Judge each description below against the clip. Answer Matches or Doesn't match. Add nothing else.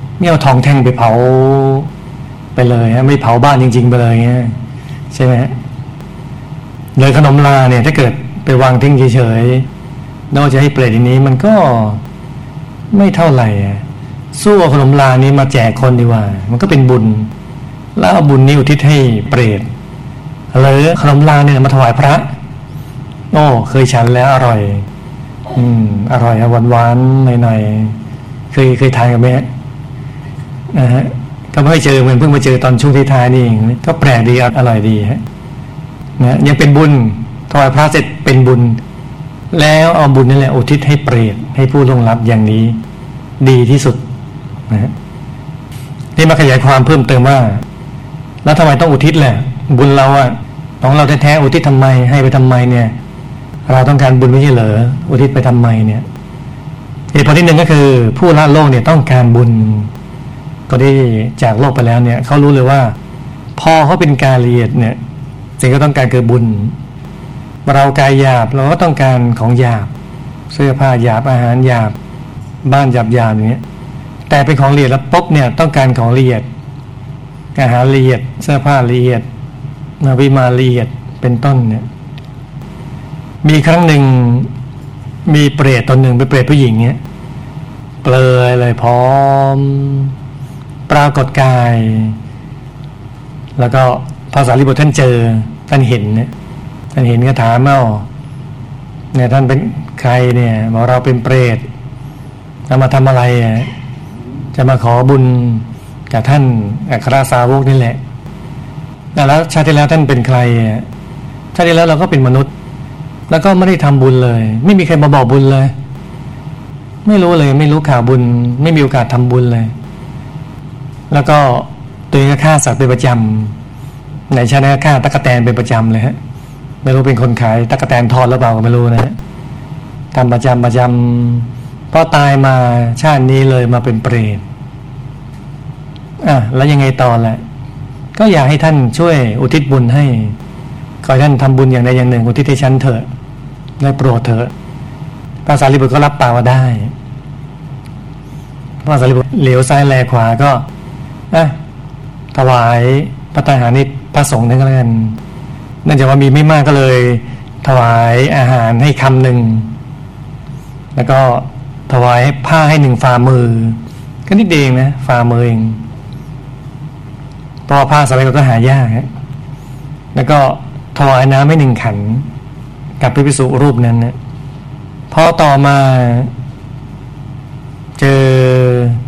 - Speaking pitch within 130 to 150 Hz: Matches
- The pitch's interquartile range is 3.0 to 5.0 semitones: Doesn't match